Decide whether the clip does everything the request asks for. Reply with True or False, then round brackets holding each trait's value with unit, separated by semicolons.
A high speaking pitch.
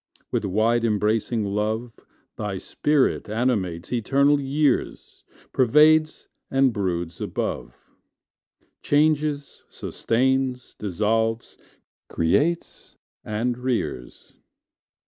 False (120 Hz)